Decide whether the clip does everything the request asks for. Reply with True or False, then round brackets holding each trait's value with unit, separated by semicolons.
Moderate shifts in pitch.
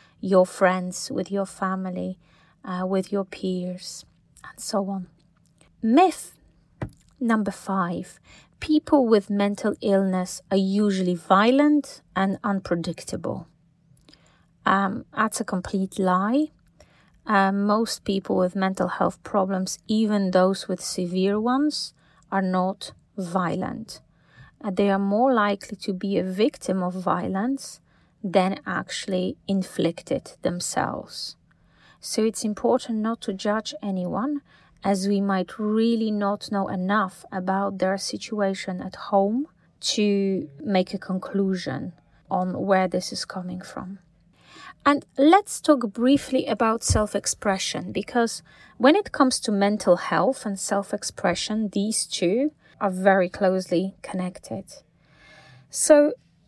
True (3.0 semitones)